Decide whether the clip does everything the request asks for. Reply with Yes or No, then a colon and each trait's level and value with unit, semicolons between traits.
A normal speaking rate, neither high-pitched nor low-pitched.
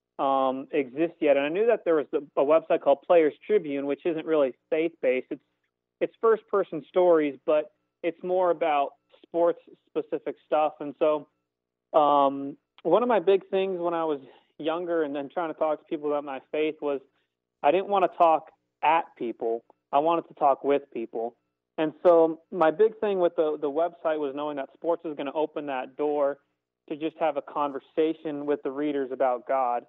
Yes: average, 195 wpm; medium, 155 Hz